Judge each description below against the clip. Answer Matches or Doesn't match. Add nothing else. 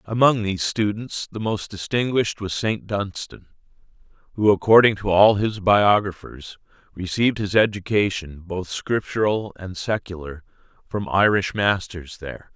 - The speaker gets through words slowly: Matches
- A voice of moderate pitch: Doesn't match